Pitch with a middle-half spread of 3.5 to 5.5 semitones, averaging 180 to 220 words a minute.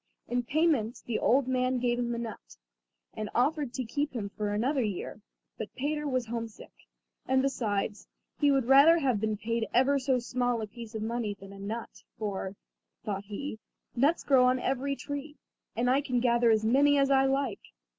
Yes: average, 3.8 semitones; average, 190 wpm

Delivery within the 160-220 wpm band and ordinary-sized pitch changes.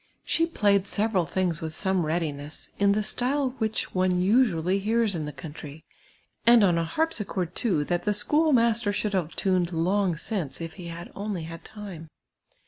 Yes: average, 170 wpm; average, 4.4 semitones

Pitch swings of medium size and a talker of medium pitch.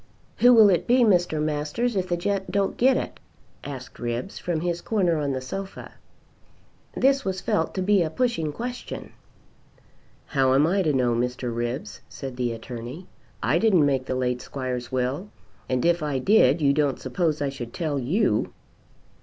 No: wide, 6.7 semitones; medium, 155 Hz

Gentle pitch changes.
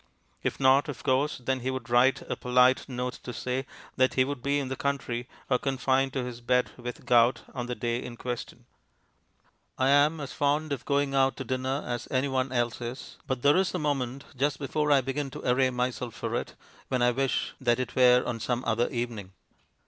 Yes: narrow, 1.9 semitones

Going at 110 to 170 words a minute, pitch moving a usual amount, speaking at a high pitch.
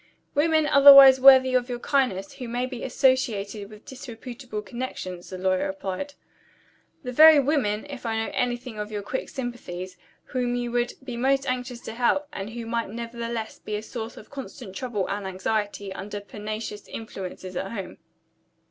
Yes: average, 165 wpm; average, 3.8 semitones; high, 235 Hz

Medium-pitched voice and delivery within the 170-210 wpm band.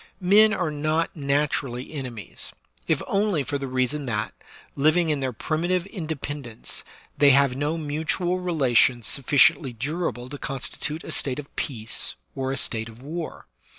No: medium, 145 Hz; average, 150 wpm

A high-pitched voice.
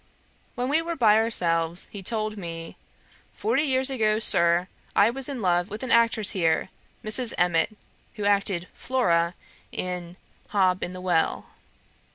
Yes: high, 205 Hz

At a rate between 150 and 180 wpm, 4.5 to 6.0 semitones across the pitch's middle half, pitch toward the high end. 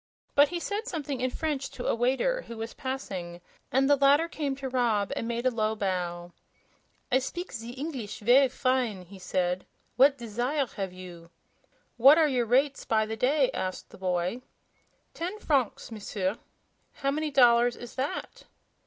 Yes: average, 170 wpm; average, 4.8 semitones; high, 245 Hz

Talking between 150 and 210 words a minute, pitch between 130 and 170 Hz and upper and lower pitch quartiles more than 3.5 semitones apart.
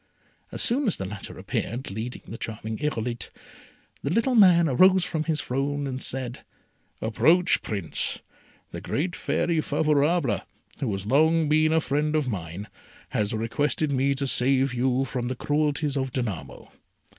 Yes: average, 155 wpm; low, 135 Hz; average, 4.8 semitones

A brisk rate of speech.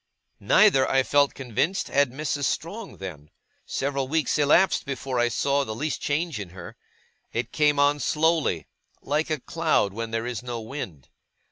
No: average, 160 wpm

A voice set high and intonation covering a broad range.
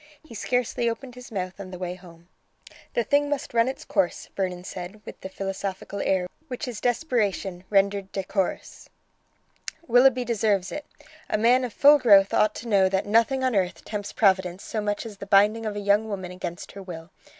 No: high, 205 Hz; average, 3.8 semitones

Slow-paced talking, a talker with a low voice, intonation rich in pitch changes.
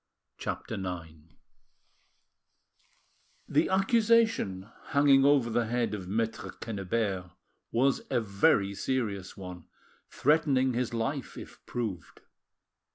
Yes: slow, 95 wpm; low, 115 Hz; wide, 5.8 semitones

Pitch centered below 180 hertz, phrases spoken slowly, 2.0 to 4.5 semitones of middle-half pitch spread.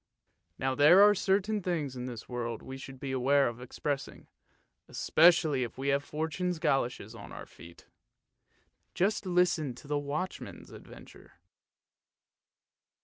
No: medium, 140 Hz; slow, 130 wpm; wide, 5.4 semitones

